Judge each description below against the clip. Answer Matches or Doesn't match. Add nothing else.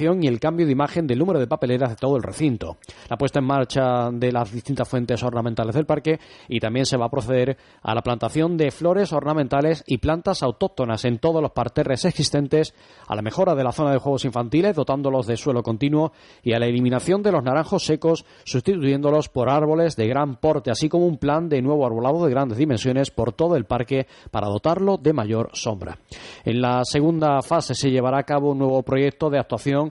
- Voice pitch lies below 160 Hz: Matches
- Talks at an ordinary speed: Doesn't match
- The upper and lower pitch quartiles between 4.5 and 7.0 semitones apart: Doesn't match